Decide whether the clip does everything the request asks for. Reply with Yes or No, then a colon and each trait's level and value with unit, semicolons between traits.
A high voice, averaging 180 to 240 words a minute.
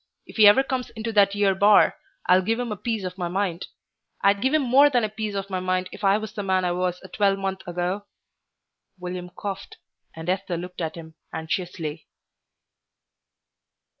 Yes: high, 195 Hz; average, 190 wpm